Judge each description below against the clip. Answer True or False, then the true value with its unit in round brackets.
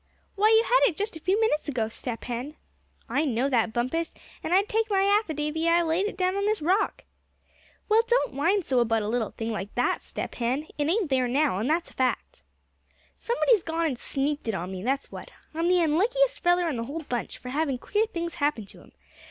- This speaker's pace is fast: True (220 wpm)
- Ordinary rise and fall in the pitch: False (7.5 semitones)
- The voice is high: True (310 Hz)